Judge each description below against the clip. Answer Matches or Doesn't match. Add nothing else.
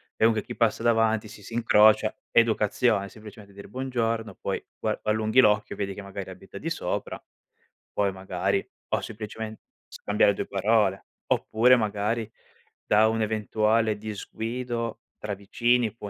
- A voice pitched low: Matches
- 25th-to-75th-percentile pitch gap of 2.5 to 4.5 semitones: Doesn't match